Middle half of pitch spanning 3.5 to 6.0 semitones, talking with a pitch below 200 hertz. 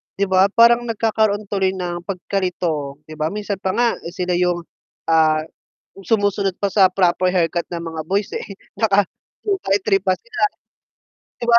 No: average, 2.9 semitones; high, 190 Hz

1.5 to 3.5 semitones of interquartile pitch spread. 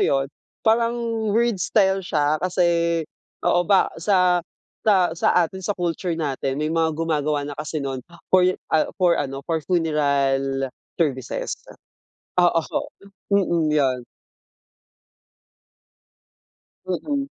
No: average, 4.2 semitones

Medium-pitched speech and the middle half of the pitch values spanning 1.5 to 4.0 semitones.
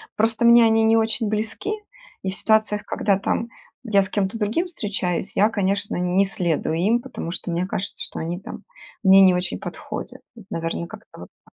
No: high, 200 Hz; average, 3.3 semitones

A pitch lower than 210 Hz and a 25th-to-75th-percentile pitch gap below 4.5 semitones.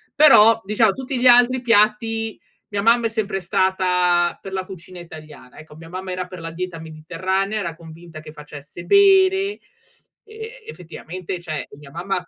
No: medium, 185 Hz; average, 5.3 semitones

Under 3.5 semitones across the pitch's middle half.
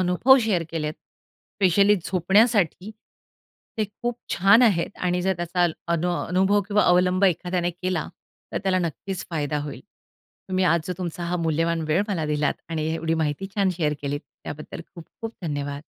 Yes: average, 3.0 semitones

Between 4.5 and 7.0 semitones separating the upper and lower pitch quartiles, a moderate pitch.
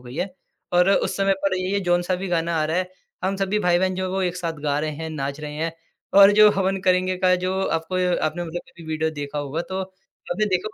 No: average, 2.7 semitones; medium, 180 Hz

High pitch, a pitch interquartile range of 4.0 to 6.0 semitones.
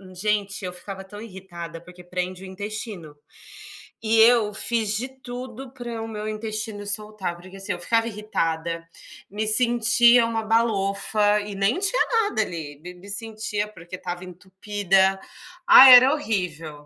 No: high, 205 Hz; average, 3.5 semitones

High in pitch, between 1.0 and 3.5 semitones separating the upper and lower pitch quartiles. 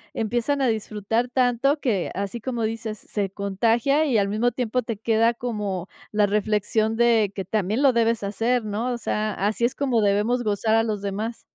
Yes: high, 225 Hz; narrow, 2.6 semitones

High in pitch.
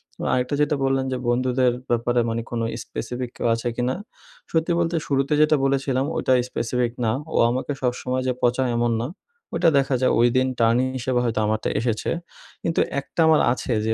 No: low, 125 Hz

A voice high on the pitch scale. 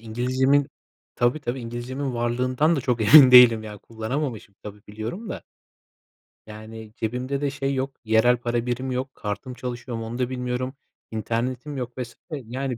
No: low, 125 Hz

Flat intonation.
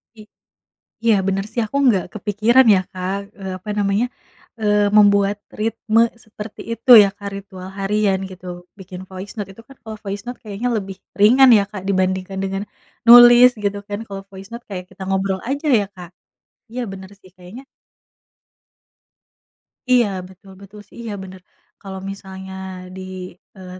Yes: narrow, 2.3 semitones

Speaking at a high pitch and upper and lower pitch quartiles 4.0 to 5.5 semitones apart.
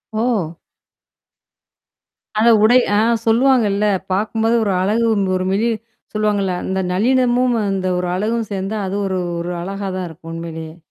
No: high, 205 Hz; average, 3.6 semitones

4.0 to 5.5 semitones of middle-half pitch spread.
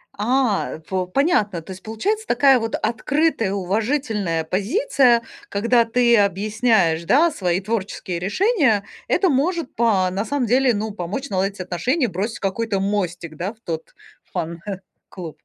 Yes: average, 5.1 semitones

